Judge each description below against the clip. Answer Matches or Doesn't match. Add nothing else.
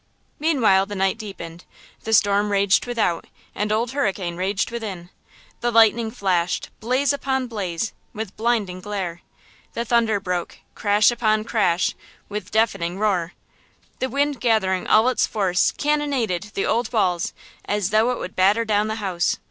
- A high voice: Matches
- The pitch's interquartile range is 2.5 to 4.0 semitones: Matches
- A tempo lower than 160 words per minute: Matches